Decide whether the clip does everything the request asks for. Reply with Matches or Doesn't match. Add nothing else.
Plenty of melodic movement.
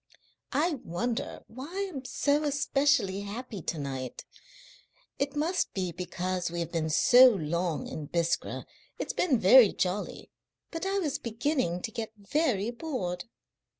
Matches